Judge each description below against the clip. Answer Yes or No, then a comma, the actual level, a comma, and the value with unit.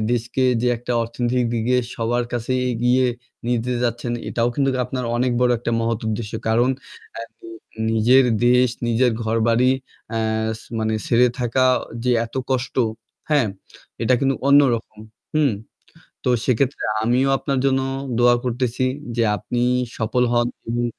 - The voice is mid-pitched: No, low, 120 Hz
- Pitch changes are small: Yes, narrow, 1.8 semitones